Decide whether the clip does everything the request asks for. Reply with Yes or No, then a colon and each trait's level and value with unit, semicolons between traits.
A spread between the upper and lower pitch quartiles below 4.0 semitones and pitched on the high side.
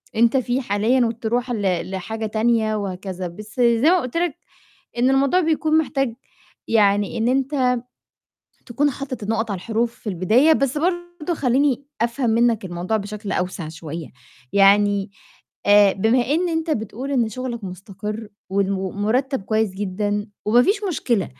No: average, 4.6 semitones; high, 225 Hz